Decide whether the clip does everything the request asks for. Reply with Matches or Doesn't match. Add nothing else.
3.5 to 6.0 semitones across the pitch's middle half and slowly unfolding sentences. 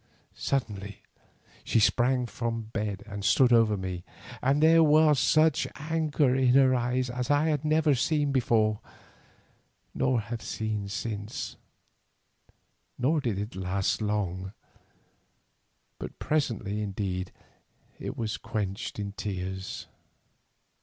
Matches